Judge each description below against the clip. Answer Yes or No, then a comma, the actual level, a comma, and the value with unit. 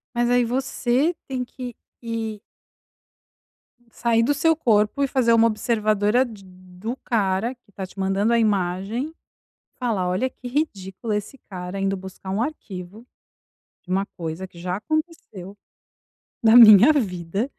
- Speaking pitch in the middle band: No, high, 220 Hz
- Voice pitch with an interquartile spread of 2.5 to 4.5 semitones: Yes, average, 4.2 semitones